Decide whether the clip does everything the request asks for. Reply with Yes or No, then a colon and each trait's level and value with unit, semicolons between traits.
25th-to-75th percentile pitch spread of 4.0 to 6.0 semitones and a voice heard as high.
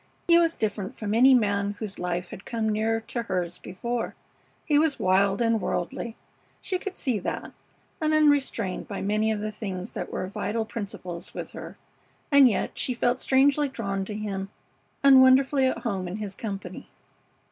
Yes: average, 4.8 semitones; high, 220 Hz